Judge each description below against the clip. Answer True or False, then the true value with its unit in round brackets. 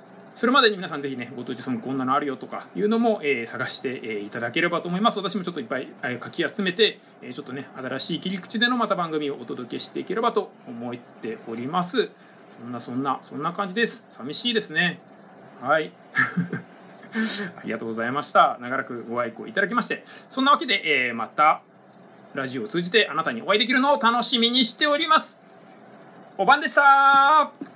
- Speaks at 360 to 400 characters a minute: True (395 characters per minute)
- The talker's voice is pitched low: False (195 Hz)